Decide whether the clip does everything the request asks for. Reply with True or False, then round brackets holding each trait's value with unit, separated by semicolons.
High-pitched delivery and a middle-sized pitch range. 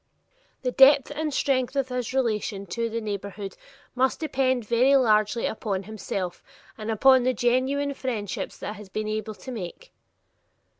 True (235 Hz; 3.8 semitones)